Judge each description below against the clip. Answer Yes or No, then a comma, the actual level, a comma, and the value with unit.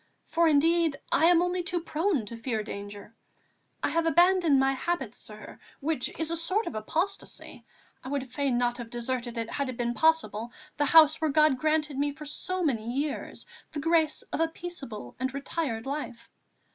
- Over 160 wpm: Yes, average, 180 wpm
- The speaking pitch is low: No, very high, 285 Hz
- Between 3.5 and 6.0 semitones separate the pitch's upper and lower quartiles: Yes, average, 5.3 semitones